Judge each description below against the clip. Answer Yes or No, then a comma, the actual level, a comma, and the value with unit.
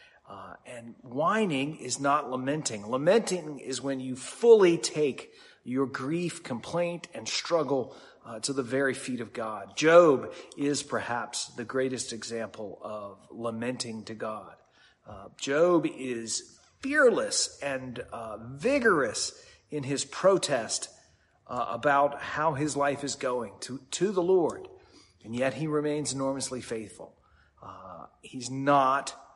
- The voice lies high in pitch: No, medium, 140 Hz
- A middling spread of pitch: Yes, average, 4.7 semitones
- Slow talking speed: Yes, slow, 130 wpm